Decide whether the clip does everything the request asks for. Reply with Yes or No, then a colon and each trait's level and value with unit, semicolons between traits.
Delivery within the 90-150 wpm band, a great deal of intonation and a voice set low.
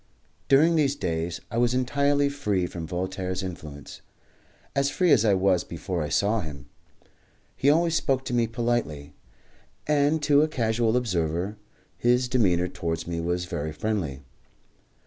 Yes: average, 145 wpm; wide, 7.8 semitones; low, 110 Hz